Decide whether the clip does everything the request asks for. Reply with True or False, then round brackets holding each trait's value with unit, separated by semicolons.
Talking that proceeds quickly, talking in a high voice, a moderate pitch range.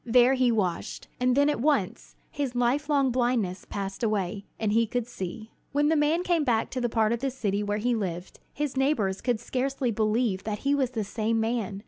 True (210 wpm; 235 Hz; 3.9 semitones)